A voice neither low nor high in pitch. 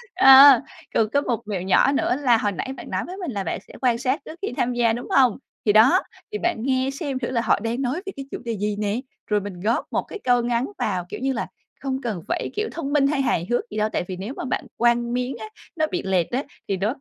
No: high, 245 Hz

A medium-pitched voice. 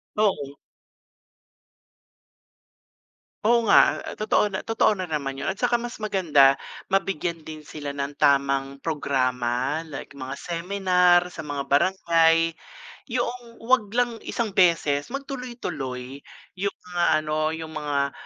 Yes: medium, 165 Hz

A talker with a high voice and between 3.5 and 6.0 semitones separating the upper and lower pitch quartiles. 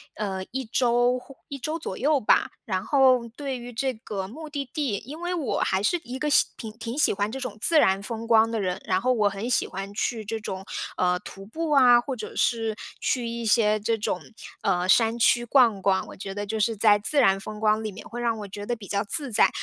Yes: high, 225 Hz; average, 3.8 semitones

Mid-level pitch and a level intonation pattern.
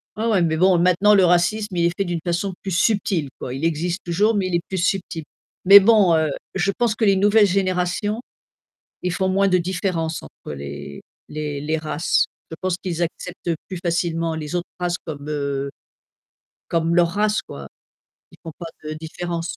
No: medium, 175 Hz; average, 3.0 semitones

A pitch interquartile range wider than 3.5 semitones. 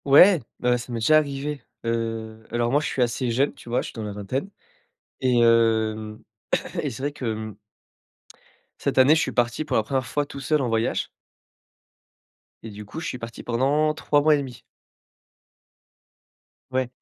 Yes: average, 3.9 semitones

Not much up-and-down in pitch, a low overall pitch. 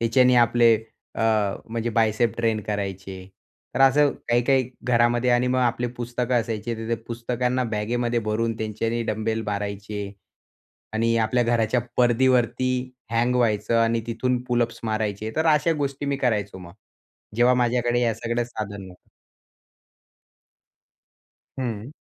Yes: narrow, 1.9 semitones; low, 115 Hz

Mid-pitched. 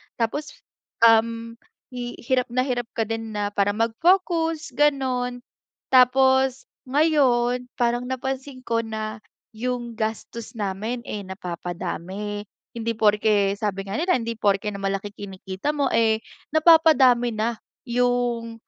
No: high, 235 Hz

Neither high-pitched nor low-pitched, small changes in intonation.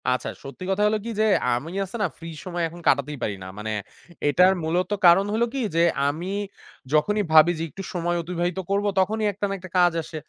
No: medium, 175 Hz; average, 3.6 semitones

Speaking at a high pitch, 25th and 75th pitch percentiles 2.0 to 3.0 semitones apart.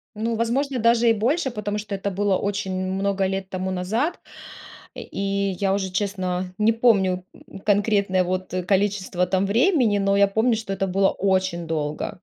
Yes: high, 200 Hz; narrow, 2.4 semitones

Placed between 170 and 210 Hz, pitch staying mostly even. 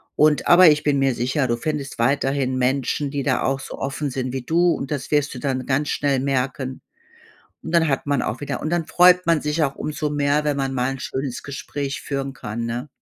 No: medium, 140 Hz; narrow, 2.2 semitones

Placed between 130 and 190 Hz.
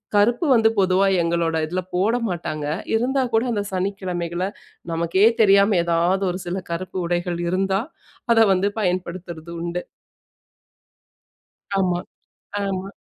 Yes: medium, 185 Hz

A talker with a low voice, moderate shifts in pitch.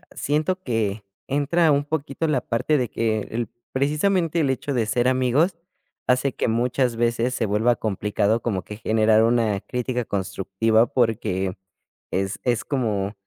Yes: low, 120 Hz; average, 4.1 semitones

